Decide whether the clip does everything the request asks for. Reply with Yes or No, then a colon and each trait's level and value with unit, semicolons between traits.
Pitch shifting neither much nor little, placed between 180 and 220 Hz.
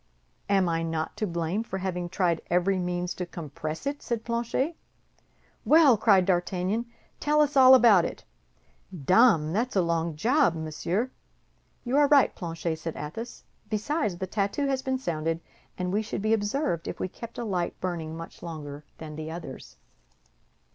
No: wide, 6.0 semitones; medium, 185 Hz